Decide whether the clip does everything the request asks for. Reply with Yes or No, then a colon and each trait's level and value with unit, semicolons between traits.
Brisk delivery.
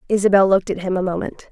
Yes: fast, 235 wpm